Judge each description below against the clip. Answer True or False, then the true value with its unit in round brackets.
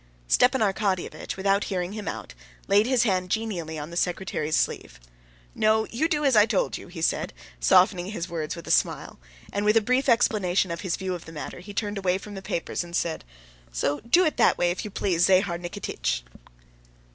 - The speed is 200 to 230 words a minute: True (205 wpm)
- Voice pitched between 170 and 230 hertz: True (190 Hz)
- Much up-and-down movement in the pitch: False (3.8 semitones)